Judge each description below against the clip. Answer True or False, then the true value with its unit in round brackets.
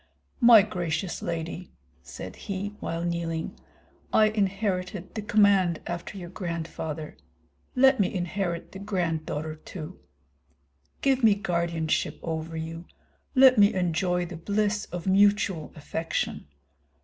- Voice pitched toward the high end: False (180 Hz)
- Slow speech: True (115 wpm)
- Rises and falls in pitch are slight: False (3.6 semitones)